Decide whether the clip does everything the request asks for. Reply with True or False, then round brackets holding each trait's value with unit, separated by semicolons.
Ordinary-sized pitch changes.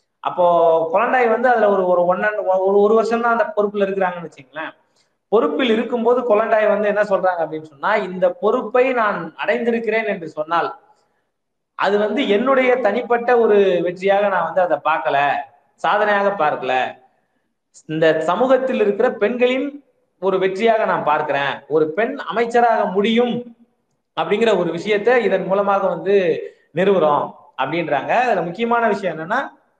True (4.5 semitones)